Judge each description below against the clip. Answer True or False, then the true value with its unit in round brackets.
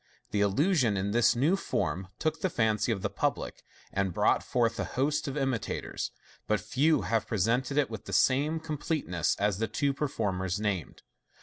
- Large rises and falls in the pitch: True (5.7 semitones)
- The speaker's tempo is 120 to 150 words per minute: False (180 wpm)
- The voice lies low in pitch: True (115 Hz)